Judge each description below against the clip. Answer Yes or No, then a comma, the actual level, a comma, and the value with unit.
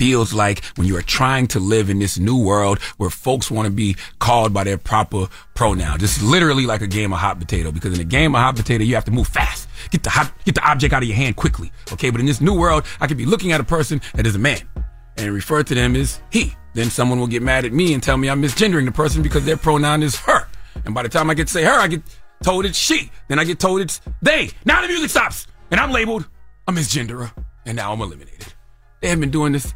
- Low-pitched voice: Yes, low, 125 Hz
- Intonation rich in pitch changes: Yes, wide, 6.3 semitones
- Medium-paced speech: No, fast, 270 wpm